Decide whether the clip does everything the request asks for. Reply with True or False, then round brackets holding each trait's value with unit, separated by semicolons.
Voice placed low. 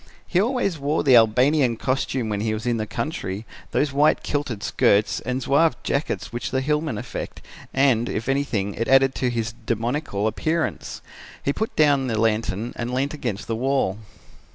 True (125 Hz)